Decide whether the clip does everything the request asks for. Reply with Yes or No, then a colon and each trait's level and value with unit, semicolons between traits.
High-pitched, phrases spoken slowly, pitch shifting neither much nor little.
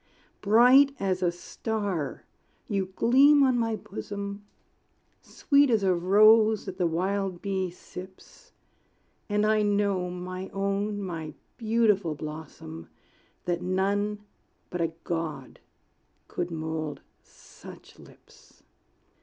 Yes: high, 195 Hz; slow, 110 wpm; average, 3.3 semitones